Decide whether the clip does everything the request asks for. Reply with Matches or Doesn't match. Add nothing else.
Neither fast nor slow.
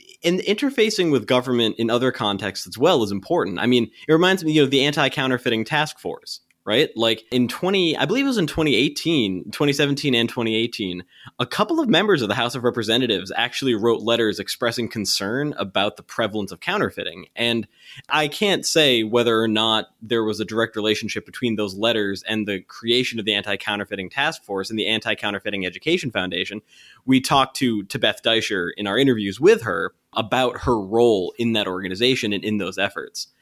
Matches